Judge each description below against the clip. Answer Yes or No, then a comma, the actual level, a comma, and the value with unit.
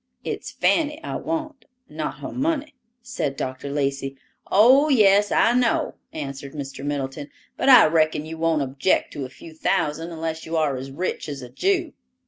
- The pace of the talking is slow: No, average, 170 wpm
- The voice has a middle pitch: Yes, medium, 160 Hz